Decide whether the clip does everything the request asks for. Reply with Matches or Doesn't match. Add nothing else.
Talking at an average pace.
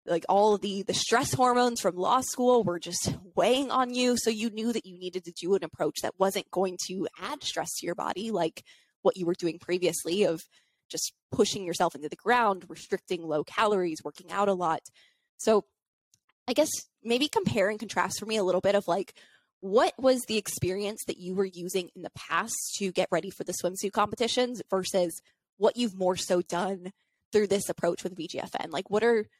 Doesn't match